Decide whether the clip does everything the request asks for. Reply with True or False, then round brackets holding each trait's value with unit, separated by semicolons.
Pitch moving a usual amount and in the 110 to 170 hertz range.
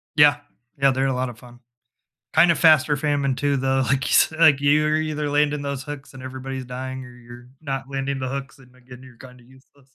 False (2.0 semitones; 135 Hz)